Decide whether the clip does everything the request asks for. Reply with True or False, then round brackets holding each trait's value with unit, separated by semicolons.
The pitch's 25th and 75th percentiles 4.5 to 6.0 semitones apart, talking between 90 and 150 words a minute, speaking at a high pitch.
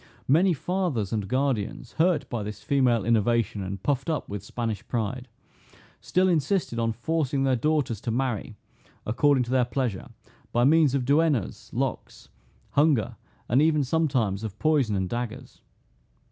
False (5.0 semitones; 145 wpm; 125 Hz)